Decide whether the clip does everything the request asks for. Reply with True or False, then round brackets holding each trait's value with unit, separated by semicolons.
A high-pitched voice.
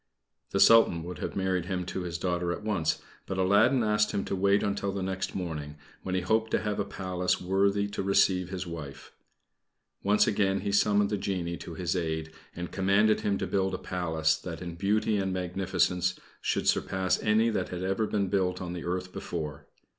False (95 Hz)